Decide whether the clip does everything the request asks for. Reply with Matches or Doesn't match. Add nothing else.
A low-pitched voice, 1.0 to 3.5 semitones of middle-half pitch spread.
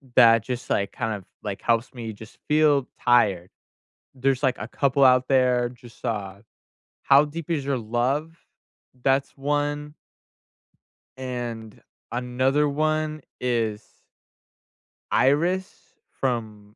Doesn't match